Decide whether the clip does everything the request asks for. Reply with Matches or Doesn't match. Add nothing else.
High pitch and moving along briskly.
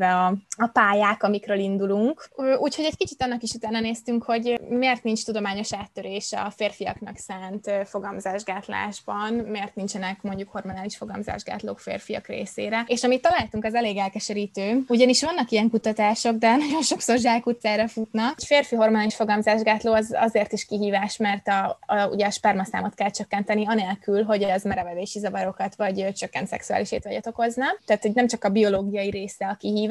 Matches